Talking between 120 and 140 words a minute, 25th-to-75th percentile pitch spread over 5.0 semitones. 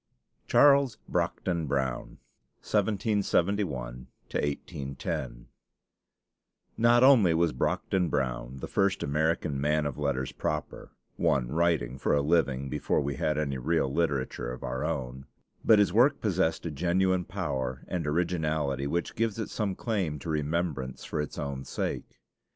Yes: slow, 135 wpm; wide, 5.4 semitones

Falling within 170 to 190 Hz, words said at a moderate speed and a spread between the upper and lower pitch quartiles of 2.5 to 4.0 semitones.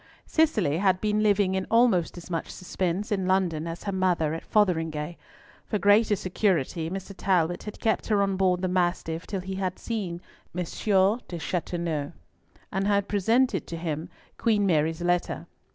Yes: medium, 185 Hz; average, 160 wpm; average, 3.0 semitones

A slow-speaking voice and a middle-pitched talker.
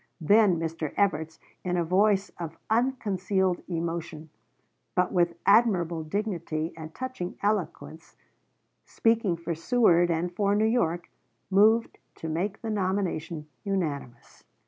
Yes: slow, 120 wpm; medium, 180 Hz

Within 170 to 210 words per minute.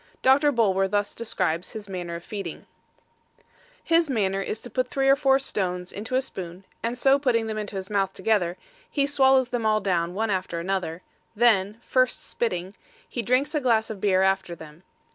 Yes: average, 185 wpm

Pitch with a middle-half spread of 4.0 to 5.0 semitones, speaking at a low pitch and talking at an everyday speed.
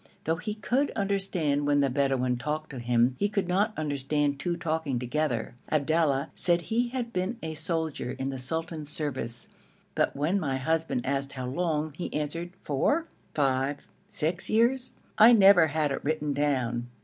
No: average, 4.5 semitones; medium, 155 Hz; average, 170 wpm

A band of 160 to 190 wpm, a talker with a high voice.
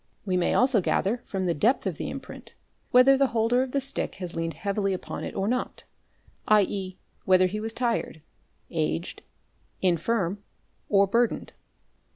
Yes: average, 165 wpm; high, 200 Hz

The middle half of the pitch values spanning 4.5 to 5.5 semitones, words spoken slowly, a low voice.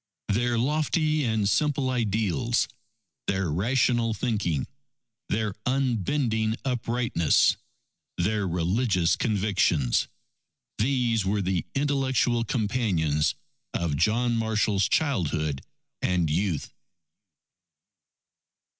Yes: average, 5.1 semitones; slow, 80 wpm; low, 110 Hz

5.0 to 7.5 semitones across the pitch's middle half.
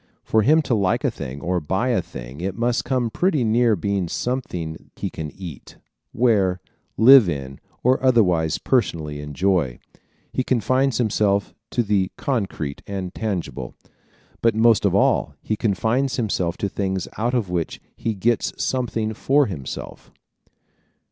Yes: wide, 5.4 semitones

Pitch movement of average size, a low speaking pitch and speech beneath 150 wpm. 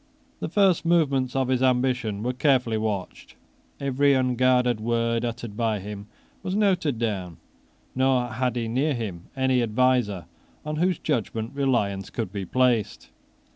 Yes: average, 3.2 semitones; low, 125 Hz; average, 140 wpm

